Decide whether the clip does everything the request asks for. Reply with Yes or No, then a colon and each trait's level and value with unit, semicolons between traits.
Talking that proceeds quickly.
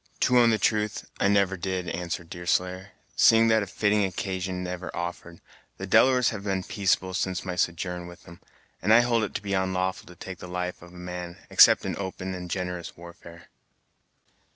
No: average, 185 wpm